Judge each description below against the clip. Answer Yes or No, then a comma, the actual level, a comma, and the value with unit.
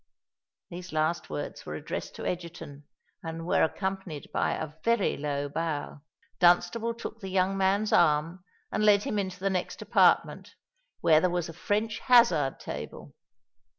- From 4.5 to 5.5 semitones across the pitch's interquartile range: No, average, 3.8 semitones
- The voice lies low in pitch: No, medium, 180 Hz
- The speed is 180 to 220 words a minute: No, average, 150 wpm